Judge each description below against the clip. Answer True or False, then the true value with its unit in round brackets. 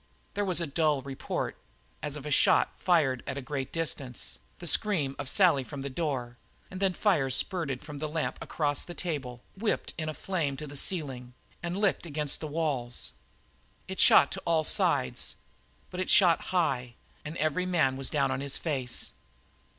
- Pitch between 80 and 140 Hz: False (150 Hz)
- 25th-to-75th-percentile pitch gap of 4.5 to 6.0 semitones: False (4.1 semitones)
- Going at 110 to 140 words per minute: False (185 wpm)